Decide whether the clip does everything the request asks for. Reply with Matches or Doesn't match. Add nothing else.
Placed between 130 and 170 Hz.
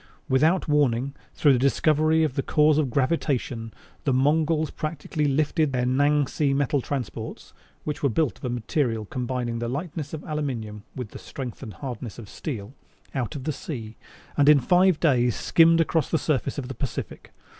Matches